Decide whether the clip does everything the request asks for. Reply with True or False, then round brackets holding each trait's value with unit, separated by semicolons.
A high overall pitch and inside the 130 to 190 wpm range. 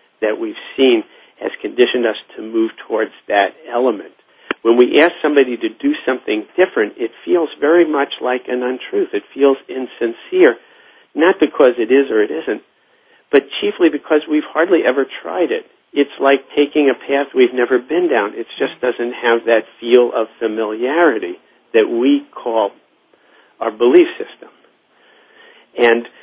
False (165 Hz; 155 wpm)